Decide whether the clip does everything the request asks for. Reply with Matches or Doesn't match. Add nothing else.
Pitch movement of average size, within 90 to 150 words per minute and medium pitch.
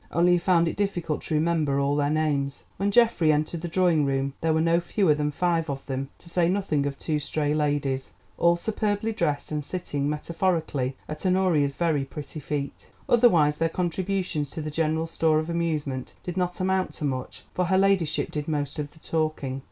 Doesn't match